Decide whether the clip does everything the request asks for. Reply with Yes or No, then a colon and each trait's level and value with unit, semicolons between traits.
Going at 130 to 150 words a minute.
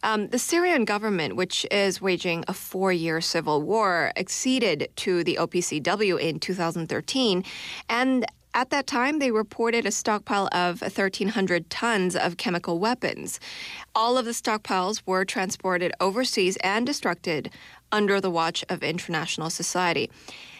Yes: slow, 135 wpm